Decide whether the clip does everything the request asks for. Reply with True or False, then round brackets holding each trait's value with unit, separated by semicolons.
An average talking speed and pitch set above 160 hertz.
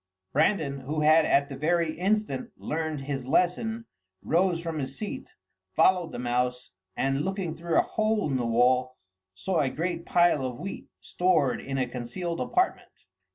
False (160 wpm; 155 Hz)